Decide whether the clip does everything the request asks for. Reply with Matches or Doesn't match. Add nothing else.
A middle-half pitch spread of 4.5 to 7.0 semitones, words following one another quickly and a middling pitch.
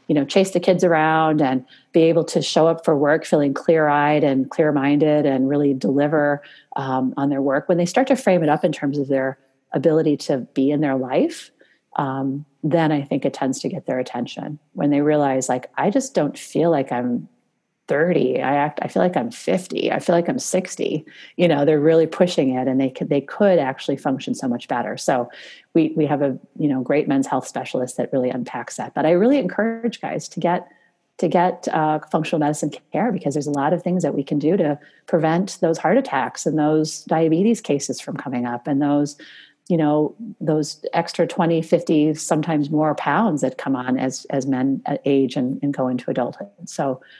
Doesn't match